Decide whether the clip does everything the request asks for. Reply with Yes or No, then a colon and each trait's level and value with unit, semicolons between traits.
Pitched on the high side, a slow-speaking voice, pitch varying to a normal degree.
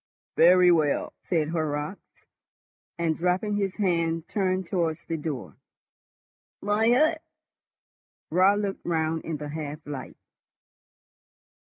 No: medium, 170 Hz; slow, 110 wpm; average, 3.5 semitones